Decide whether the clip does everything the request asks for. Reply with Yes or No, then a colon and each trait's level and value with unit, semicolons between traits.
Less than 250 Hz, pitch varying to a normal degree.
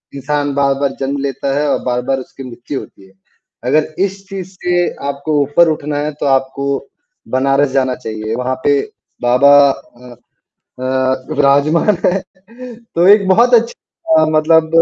Yes: medium, 140 Hz; average, 3.1 semitones